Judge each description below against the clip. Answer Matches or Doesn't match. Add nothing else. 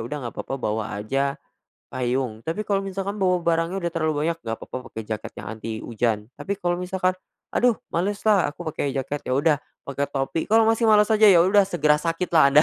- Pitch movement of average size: Doesn't match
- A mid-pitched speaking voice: Matches